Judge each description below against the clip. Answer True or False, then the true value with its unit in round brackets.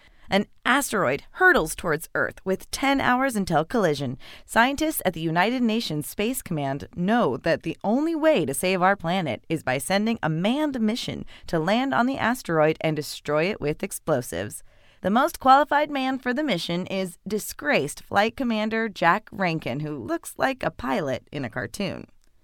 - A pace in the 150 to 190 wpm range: True (170 wpm)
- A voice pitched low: False (200 Hz)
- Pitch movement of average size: False (7.2 semitones)